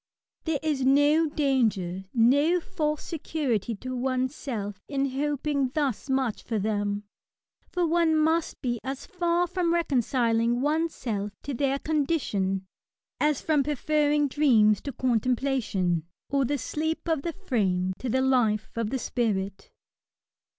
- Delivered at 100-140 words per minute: Yes, slow, 135 wpm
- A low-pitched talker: No, very high, 265 Hz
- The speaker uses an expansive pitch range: No, average, 5.0 semitones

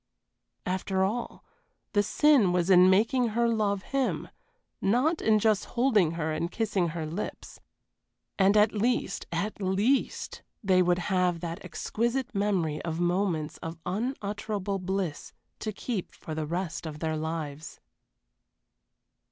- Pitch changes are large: No, average, 4.2 semitones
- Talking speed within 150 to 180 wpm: No, slow, 135 wpm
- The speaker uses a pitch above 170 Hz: Yes, high, 190 Hz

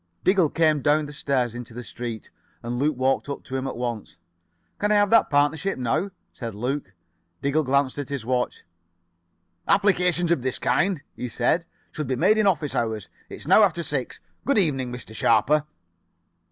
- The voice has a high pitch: No, medium, 140 Hz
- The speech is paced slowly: No, average, 180 wpm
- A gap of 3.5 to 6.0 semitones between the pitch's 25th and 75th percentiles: Yes, average, 5.2 semitones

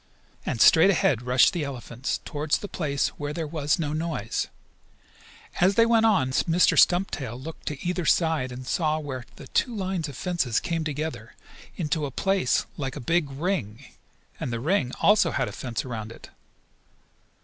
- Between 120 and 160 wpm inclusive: No, average, 170 wpm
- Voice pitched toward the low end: No, medium, 150 Hz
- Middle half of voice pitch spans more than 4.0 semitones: Yes, average, 5.2 semitones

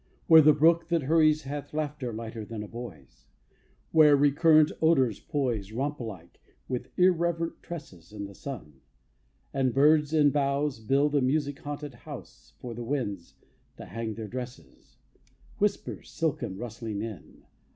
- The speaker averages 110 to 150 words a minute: Yes, average, 145 wpm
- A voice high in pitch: No, medium, 140 Hz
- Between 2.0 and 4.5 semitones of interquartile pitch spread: No, average, 5.1 semitones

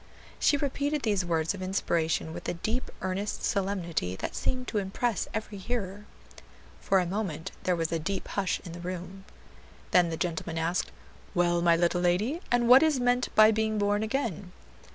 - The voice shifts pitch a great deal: No, average, 4.1 semitones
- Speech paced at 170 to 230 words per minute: Yes, average, 180 wpm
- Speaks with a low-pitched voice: No, high, 190 Hz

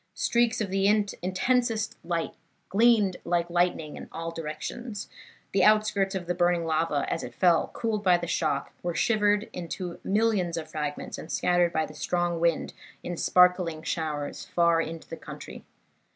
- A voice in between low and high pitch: Yes, medium, 175 Hz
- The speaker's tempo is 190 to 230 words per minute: No, average, 160 wpm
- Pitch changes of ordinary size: Yes, average, 3.6 semitones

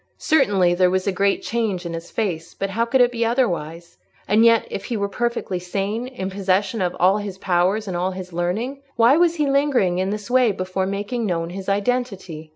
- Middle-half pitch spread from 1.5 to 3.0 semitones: No, average, 4.2 semitones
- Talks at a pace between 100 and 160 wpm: No, fast, 205 wpm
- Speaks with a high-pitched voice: Yes, high, 200 Hz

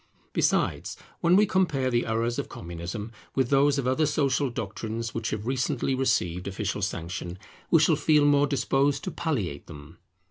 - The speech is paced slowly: No, average, 165 wpm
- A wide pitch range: Yes, wide, 5.9 semitones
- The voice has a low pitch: Yes, low, 125 Hz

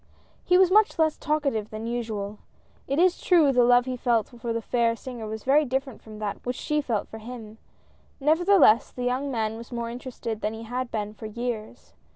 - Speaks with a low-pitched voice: No, high, 240 Hz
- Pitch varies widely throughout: No, average, 3.6 semitones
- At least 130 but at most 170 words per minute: No, average, 200 wpm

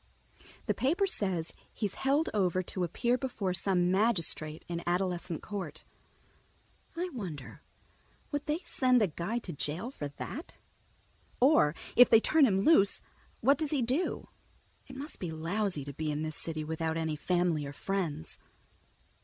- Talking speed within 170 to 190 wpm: No, average, 155 wpm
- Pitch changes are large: Yes, wide, 7.6 semitones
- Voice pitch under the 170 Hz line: No, high, 190 Hz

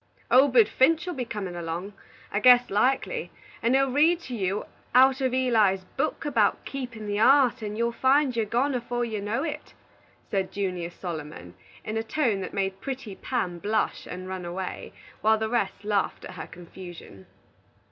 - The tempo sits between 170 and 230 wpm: Yes, average, 175 wpm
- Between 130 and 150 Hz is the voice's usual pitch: No, high, 220 Hz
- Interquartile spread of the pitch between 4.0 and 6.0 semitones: Yes, average, 5.2 semitones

